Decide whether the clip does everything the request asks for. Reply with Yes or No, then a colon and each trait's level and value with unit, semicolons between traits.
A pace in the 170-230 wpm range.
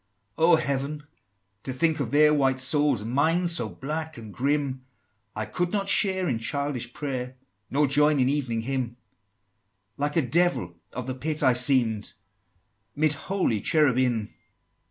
No: average, 155 wpm